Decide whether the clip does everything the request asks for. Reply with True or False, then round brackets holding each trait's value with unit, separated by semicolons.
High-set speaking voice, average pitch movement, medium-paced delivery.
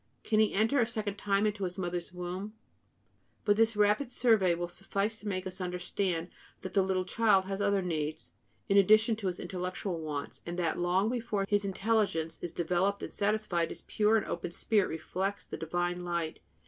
True (195 Hz; 3.0 semitones; 185 wpm)